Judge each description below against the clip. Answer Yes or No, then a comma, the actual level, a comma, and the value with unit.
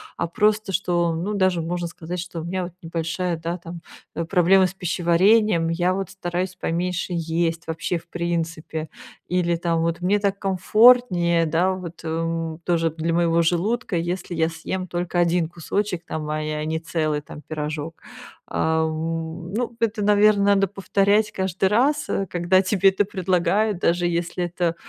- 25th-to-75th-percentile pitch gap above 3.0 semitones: No, narrow, 2.5 semitones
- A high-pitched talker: No, medium, 175 Hz